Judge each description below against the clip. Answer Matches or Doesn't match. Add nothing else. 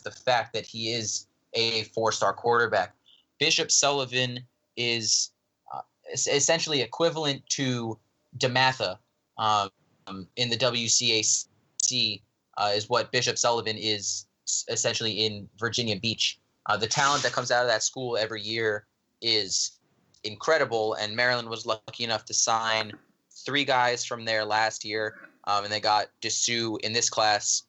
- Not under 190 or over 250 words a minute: Doesn't match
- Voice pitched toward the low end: Matches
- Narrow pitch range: Matches